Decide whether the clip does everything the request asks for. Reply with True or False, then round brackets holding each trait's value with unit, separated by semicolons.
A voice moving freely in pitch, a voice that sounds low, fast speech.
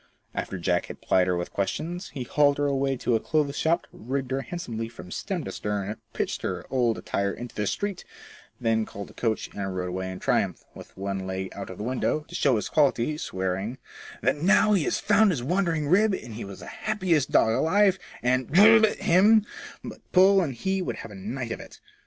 True (8.8 semitones; 130 Hz; 210 wpm)